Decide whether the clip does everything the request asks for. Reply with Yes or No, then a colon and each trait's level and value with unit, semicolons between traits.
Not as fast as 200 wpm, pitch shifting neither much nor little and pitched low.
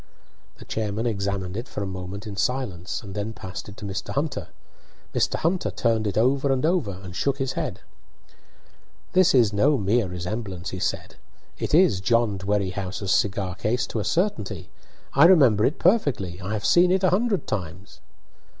No: average, 175 wpm; wide, 5.7 semitones; low, 105 Hz